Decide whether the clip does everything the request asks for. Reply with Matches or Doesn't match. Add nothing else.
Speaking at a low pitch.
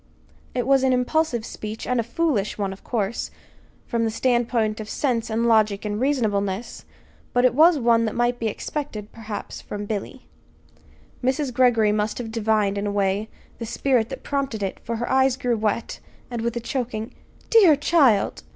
Doesn't match